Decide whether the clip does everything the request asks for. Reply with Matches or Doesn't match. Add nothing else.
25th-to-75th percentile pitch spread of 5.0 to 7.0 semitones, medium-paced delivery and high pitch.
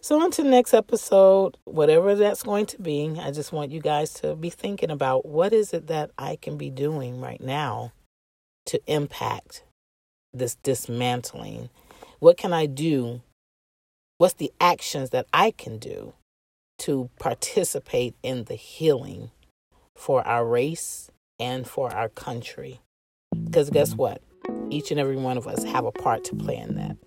Doesn't match